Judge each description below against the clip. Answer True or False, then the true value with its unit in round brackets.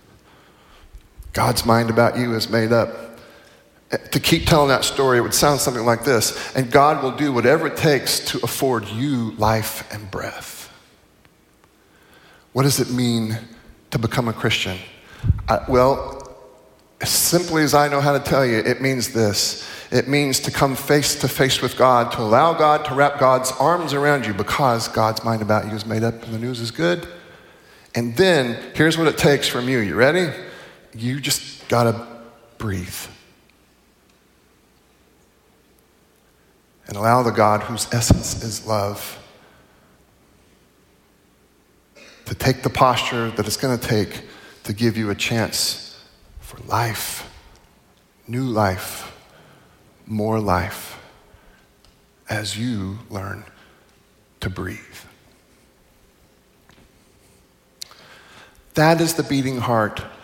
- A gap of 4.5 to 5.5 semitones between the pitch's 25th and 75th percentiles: False (3.6 semitones)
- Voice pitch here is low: True (120 Hz)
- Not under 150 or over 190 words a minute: False (135 wpm)